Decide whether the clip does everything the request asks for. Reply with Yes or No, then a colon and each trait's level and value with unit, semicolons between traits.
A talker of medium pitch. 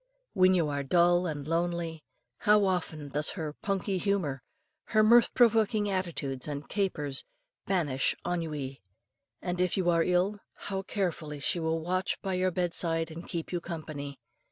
Yes: medium, 175 Hz